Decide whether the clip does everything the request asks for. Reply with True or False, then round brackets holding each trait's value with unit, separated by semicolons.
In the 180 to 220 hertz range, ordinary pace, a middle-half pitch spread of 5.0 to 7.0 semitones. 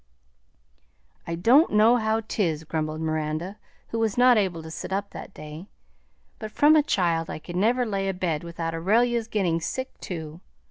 True (190 Hz; 170 wpm; 5.4 semitones)